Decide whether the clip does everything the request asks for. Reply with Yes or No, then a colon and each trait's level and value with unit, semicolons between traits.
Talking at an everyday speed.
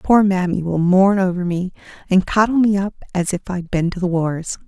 No: fast, 220 wpm